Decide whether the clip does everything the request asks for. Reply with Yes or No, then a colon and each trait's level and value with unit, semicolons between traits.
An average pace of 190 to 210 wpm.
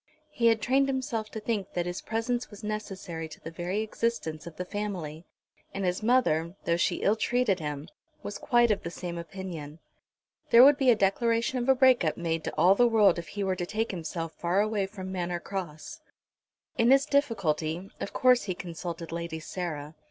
Yes: average, 195 wpm